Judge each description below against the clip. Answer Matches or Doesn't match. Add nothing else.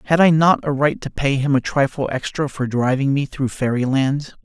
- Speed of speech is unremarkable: Doesn't match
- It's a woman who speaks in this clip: Doesn't match